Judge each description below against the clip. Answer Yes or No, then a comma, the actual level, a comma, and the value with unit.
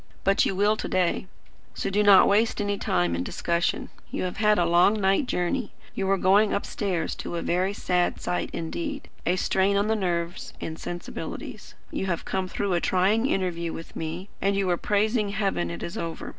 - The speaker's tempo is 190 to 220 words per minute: Yes, average, 200 wpm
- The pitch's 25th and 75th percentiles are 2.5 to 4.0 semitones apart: Yes, average, 2.8 semitones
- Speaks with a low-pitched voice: No, high, 190 Hz